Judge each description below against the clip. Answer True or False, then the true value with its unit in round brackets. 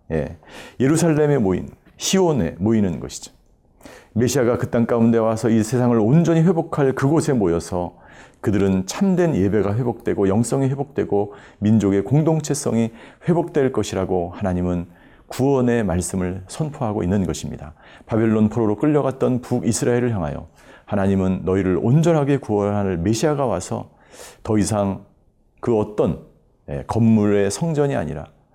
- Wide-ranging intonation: True (5.9 semitones)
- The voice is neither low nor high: False (115 Hz)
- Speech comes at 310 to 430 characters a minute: True (320 characters per minute)